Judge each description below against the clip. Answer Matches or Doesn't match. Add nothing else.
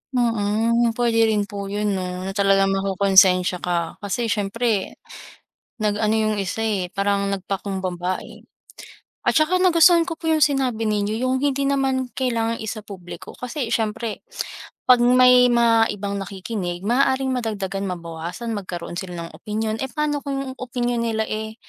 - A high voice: Matches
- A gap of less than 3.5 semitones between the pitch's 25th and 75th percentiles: Doesn't match